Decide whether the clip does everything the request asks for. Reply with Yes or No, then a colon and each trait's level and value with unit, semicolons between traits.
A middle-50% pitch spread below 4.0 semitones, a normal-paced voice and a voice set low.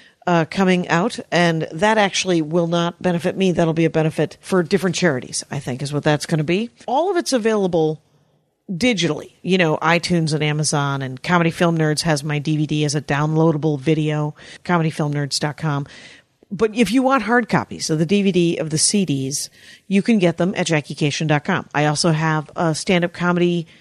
No: average, 3.2 semitones; average, 180 wpm; medium, 165 Hz